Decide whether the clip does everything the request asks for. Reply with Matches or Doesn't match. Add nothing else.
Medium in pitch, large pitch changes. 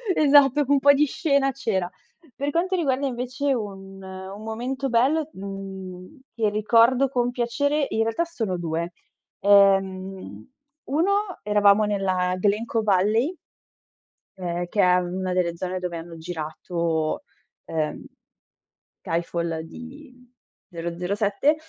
Doesn't match